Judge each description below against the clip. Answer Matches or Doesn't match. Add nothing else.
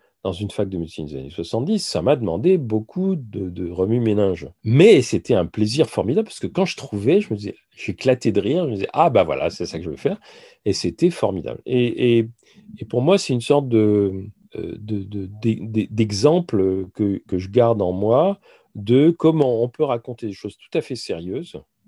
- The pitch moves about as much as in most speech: Doesn't match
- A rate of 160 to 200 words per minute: Doesn't match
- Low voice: Matches